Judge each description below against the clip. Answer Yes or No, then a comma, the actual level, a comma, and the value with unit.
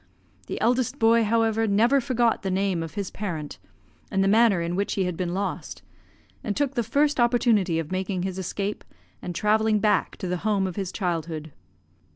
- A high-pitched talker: Yes, high, 200 Hz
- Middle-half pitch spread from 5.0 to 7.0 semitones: No, average, 3.8 semitones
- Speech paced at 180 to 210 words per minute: Yes, average, 190 wpm